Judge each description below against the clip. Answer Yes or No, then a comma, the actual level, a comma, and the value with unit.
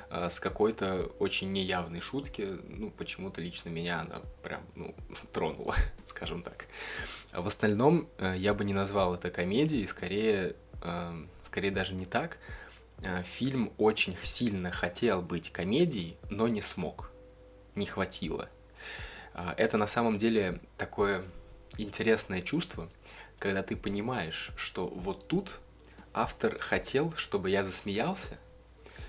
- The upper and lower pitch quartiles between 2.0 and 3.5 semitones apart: Yes, average, 3.2 semitones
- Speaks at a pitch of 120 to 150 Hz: No, low, 100 Hz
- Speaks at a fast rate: No, average, 120 wpm